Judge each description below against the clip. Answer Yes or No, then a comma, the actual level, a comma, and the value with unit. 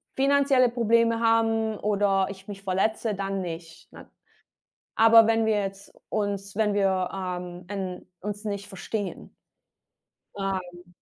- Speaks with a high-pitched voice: Yes, high, 200 Hz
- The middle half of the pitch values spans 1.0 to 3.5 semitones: Yes, average, 2.7 semitones